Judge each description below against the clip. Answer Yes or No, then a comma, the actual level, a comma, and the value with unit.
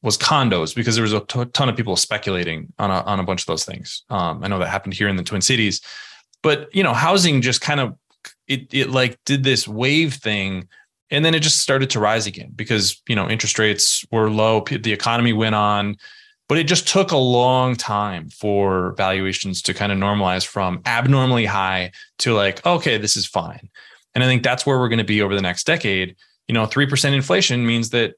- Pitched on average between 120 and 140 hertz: No, low, 110 Hz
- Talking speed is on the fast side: Yes, fast, 220 wpm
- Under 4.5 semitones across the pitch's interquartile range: No, average, 4.9 semitones